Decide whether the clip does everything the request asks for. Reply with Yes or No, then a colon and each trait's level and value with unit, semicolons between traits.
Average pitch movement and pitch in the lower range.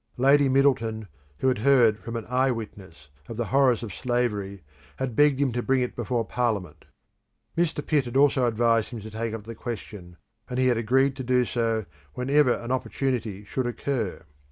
Yes: average, 3.1 semitones; low, 120 Hz